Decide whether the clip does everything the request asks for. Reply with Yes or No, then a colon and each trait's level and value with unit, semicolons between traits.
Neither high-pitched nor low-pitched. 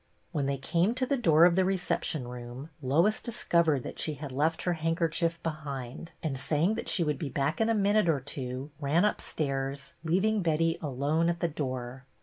Yes: medium, 155 Hz